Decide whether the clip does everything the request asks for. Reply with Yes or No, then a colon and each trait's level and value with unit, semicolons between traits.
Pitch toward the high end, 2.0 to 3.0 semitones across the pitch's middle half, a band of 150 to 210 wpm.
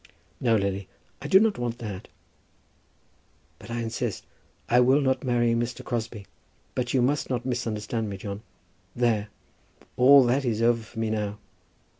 No: low, 120 Hz; narrow, 2.4 semitones; average, 155 wpm